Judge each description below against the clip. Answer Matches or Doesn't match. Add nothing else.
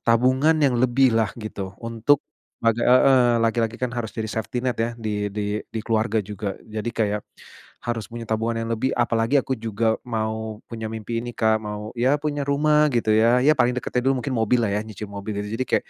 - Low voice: Matches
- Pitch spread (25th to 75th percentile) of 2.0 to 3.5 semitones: Matches